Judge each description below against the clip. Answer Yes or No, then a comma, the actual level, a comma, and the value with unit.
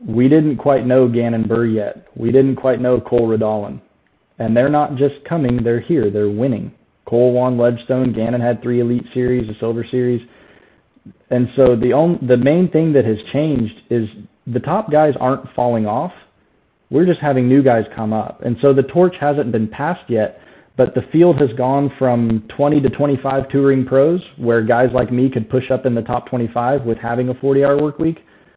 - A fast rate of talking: No, average, 195 wpm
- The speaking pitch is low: Yes, low, 125 Hz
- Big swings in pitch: No, average, 2.9 semitones